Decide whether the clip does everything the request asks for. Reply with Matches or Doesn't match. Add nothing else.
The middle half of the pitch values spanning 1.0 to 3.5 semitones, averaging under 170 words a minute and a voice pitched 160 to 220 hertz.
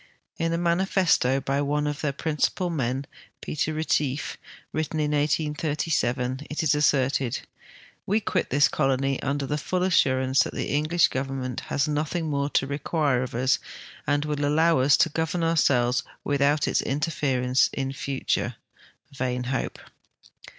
Doesn't match